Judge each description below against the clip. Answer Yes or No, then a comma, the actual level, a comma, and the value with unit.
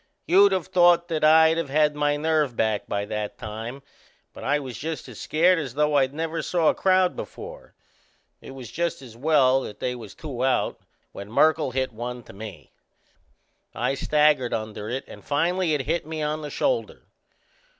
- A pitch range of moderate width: Yes, average, 4.7 semitones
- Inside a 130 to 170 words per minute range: No, average, 185 wpm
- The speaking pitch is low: No, medium, 150 Hz